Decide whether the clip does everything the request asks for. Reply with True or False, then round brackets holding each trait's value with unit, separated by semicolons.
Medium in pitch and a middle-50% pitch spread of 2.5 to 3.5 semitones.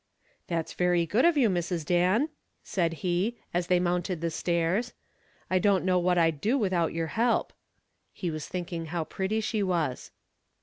True (180 Hz; 2.8 semitones)